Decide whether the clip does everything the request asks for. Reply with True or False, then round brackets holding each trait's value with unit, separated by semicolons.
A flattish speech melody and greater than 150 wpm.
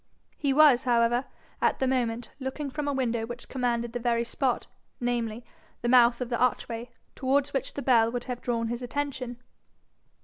True (1.9 semitones; 175 wpm)